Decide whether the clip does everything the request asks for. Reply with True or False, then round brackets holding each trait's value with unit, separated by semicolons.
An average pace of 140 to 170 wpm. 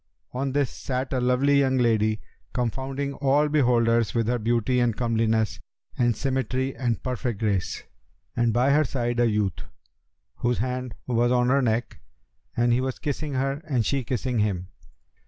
True (160 wpm)